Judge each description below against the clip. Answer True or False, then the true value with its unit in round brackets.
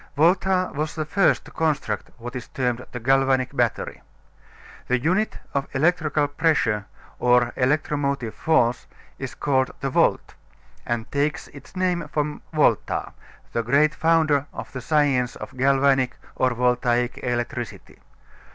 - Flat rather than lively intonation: False (3.7 semitones)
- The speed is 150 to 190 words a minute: False (135 wpm)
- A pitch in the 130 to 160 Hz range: True (135 Hz)